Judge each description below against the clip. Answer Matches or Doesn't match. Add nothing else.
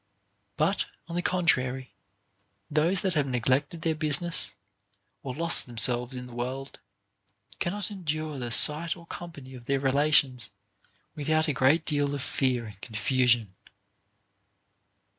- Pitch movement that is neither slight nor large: Matches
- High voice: Doesn't match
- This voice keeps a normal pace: Doesn't match